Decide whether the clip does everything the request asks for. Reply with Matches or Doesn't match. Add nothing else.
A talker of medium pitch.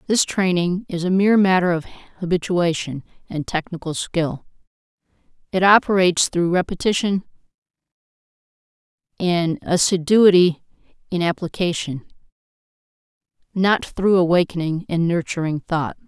Matches